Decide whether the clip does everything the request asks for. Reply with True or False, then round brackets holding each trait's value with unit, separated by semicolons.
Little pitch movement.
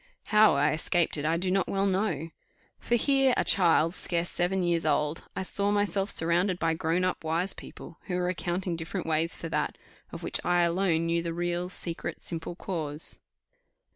True (2.3 semitones)